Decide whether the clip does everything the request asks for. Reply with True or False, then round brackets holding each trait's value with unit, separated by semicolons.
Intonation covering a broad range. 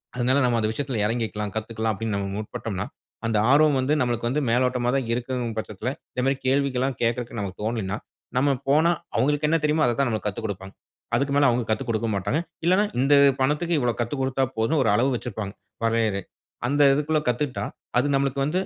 False (3.9 semitones)